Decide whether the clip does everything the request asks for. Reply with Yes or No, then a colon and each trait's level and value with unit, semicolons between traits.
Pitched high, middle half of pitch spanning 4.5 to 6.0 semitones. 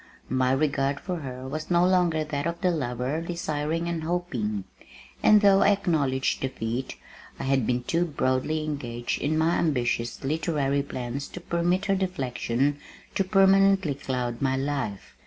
No: medium, 145 Hz; average, 4.8 semitones